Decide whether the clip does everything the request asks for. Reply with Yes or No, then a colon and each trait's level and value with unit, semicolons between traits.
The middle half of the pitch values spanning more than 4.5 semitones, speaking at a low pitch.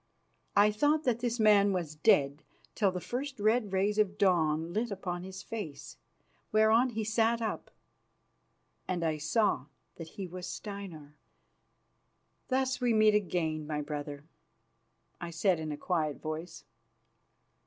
No: average, 5.3 semitones; high, 195 Hz